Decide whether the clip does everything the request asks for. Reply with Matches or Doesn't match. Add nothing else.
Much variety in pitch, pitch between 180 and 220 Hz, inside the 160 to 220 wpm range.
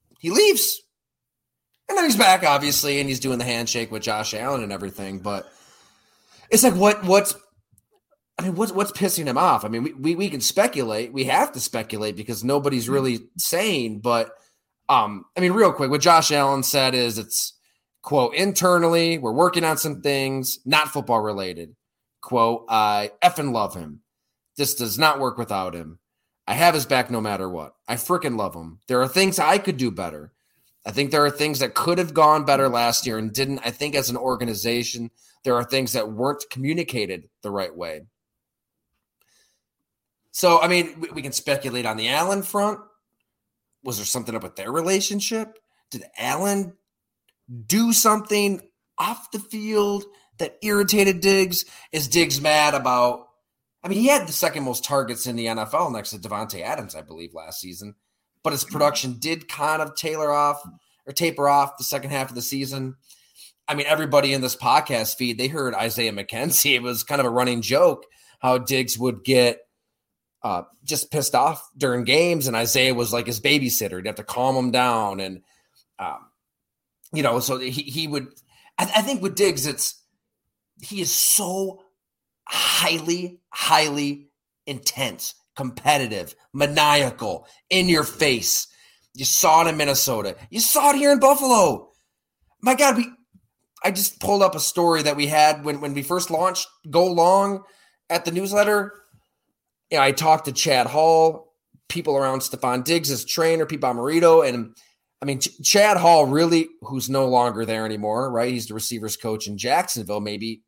Doesn't match